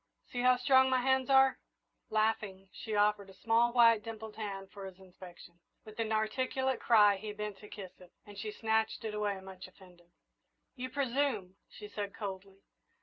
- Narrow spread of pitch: No, average, 3.5 semitones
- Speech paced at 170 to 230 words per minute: Yes, average, 175 wpm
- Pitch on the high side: Yes, high, 210 Hz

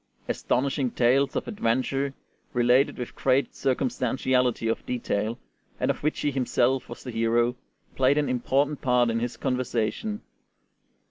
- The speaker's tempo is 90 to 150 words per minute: Yes, slow, 135 wpm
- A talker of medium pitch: No, low, 125 Hz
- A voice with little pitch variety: Yes, narrow, 2.2 semitones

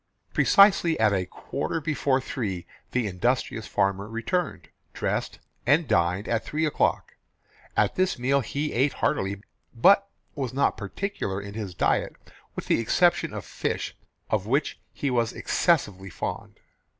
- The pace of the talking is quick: No, average, 140 wpm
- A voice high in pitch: No, low, 120 Hz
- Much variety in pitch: Yes, wide, 7.0 semitones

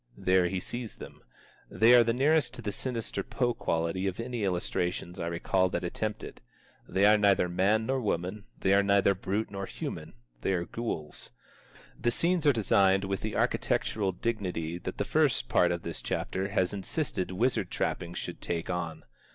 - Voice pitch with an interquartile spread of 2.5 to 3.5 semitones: No, average, 4.0 semitones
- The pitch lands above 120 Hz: No, low, 100 Hz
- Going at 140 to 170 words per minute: No, average, 180 wpm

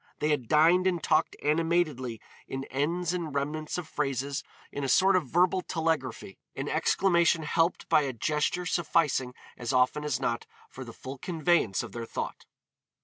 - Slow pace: No, average, 165 wpm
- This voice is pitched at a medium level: Yes, medium, 150 Hz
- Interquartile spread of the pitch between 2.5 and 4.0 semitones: No, average, 4.5 semitones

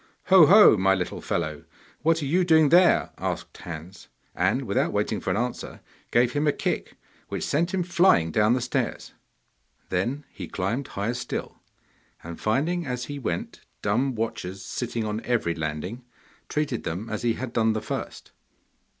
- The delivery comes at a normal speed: Yes, average, 165 wpm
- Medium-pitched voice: No, low, 120 Hz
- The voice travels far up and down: Yes, wide, 7.1 semitones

